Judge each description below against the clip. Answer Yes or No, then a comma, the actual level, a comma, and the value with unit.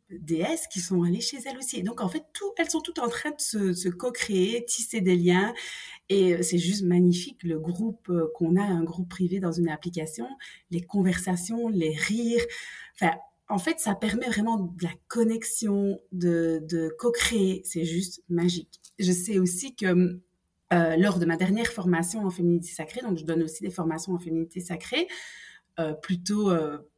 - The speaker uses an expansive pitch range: No, average, 4.3 semitones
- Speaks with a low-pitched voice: No, medium, 180 Hz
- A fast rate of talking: No, average, 180 wpm